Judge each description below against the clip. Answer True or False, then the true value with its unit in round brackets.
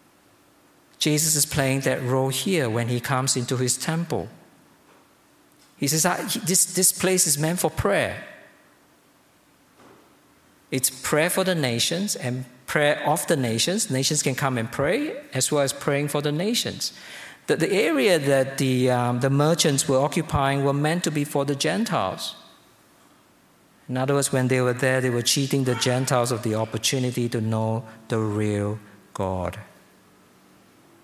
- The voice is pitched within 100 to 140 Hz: True (135 Hz)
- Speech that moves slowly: False (155 wpm)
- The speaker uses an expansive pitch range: False (3.8 semitones)